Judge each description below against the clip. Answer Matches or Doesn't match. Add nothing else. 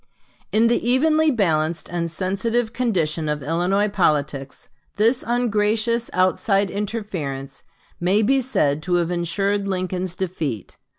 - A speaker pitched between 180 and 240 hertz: Matches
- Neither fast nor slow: Doesn't match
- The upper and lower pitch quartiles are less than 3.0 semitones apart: Doesn't match